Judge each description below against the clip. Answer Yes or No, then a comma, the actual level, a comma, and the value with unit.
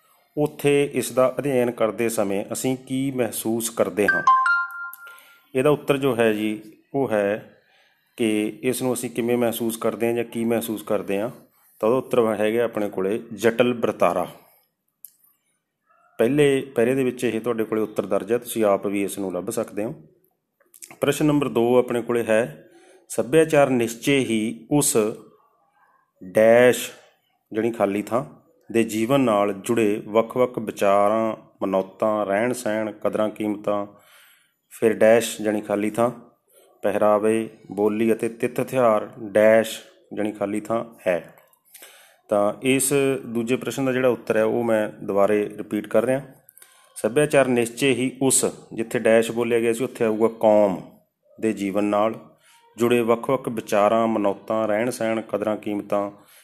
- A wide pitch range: No, average, 3.0 semitones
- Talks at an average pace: Yes, average, 135 wpm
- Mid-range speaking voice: No, low, 115 Hz